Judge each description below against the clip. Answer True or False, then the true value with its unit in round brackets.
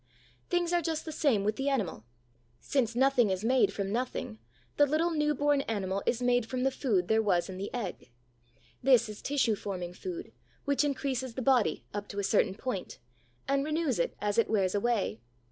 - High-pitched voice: True (240 Hz)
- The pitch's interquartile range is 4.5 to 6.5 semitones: True (5.5 semitones)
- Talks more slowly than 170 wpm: False (195 wpm)